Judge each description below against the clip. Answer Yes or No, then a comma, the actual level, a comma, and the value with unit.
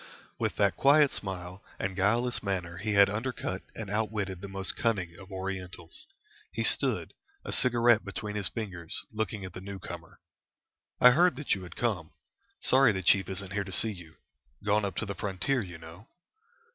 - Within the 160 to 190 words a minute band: Yes, average, 175 wpm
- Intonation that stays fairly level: No, average, 3.0 semitones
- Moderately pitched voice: No, low, 100 Hz